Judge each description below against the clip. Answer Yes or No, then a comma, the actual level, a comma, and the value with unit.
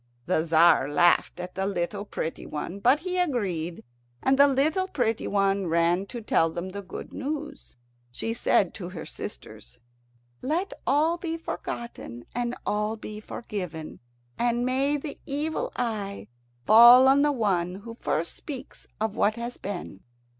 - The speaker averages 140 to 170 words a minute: Yes, average, 155 wpm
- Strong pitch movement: Yes, wide, 7.1 semitones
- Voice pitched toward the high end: Yes, high, 215 Hz